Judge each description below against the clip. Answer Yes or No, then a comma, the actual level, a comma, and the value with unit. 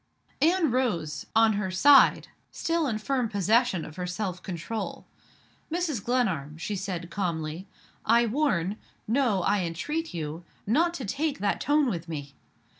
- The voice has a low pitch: No, high, 210 Hz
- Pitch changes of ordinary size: No, wide, 7.1 semitones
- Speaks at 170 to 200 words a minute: No, average, 145 wpm